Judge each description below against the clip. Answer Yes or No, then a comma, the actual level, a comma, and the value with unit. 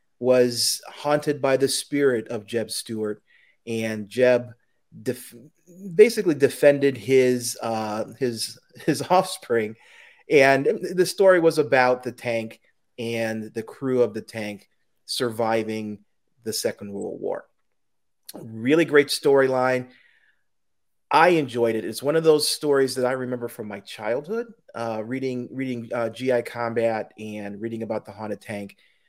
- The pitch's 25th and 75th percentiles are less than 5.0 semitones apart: Yes, average, 3.7 semitones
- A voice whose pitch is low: Yes, low, 125 Hz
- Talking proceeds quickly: No, slow, 135 wpm